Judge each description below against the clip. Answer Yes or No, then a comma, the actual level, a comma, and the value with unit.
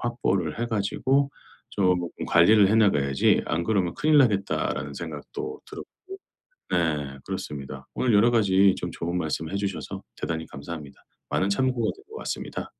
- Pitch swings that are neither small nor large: No, wide, 5.9 semitones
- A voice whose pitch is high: No, low, 100 Hz